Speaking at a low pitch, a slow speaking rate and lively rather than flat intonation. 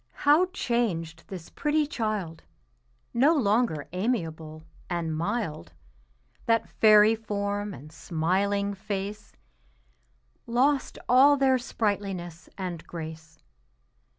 No: high, 200 Hz; slow, 95 wpm; wide, 6.0 semitones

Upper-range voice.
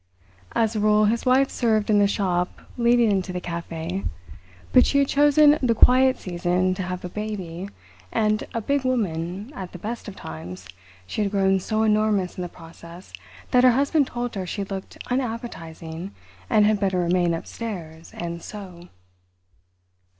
Yes: high, 200 Hz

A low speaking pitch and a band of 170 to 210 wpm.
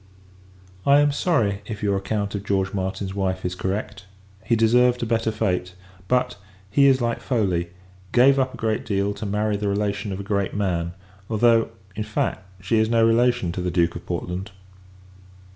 Yes: low, 105 Hz; average, 180 wpm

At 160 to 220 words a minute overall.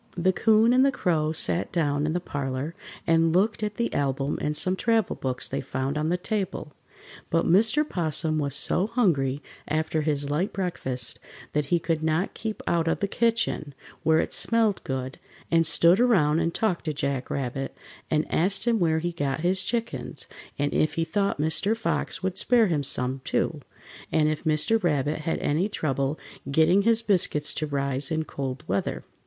Yes: average, 180 wpm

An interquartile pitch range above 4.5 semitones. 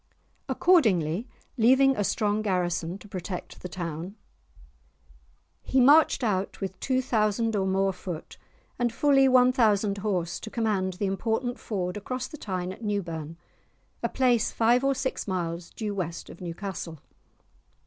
Yes: average, 4.9 semitones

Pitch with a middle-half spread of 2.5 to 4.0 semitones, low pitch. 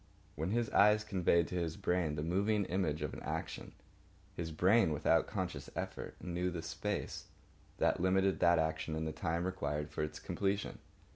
Yes: average, 3.4 semitones; very low, 85 Hz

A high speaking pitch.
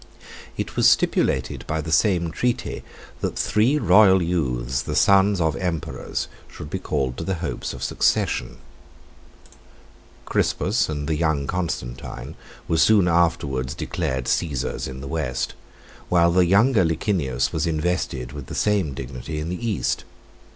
No: very low, 80 Hz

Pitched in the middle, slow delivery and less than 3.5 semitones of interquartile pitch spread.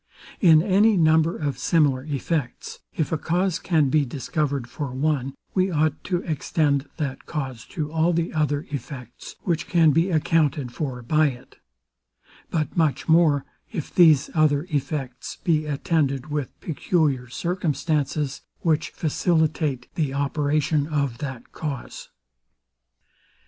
Yes: medium, 150 Hz; slow, 130 wpm; average, 2.8 semitones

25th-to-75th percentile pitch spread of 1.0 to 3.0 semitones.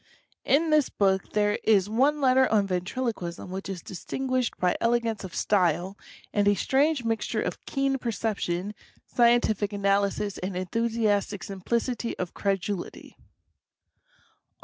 No: average, 3.8 semitones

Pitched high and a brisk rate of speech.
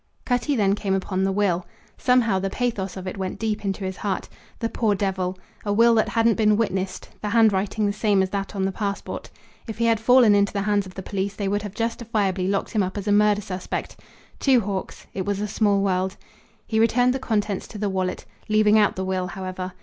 Yes: high, 205 Hz; fast, 225 wpm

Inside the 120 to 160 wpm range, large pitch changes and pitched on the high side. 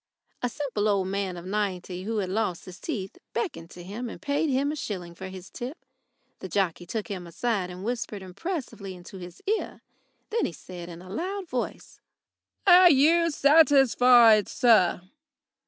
No: average, 170 wpm; wide, 6.9 semitones; high, 210 Hz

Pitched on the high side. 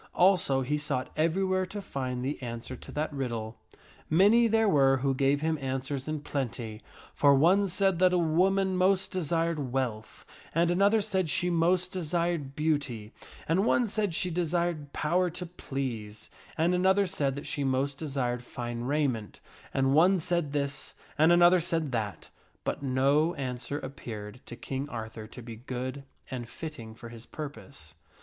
No: medium, 145 Hz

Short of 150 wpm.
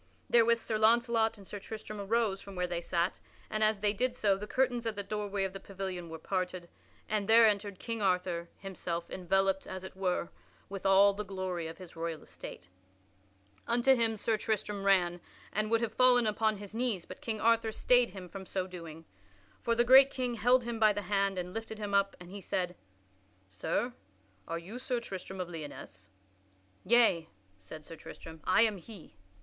No: average, 190 wpm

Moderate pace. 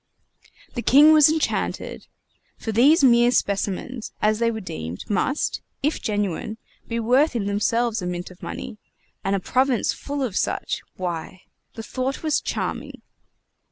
Yes: average, 150 wpm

